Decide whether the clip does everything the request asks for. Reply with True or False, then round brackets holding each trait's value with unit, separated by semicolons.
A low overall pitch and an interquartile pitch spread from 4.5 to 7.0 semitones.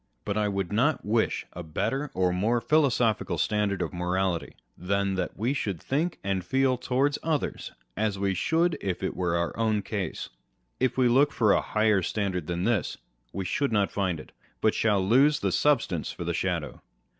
True (105 Hz; 5.3 semitones)